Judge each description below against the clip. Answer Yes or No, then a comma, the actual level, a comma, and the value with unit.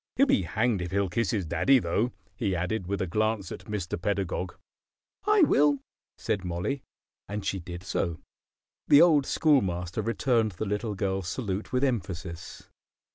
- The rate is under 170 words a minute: Yes, average, 160 wpm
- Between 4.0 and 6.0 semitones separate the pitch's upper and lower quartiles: Yes, average, 5.0 semitones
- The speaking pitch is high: No, low, 100 Hz